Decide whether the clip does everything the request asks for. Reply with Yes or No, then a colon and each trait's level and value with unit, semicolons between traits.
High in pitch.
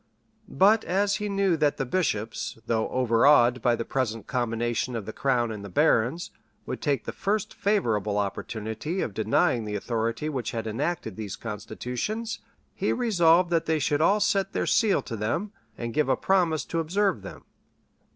No: low, 130 Hz